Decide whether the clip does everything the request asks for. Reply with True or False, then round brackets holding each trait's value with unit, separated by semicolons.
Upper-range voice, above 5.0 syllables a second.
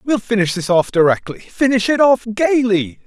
False (215 Hz; 4.9 syllables/s)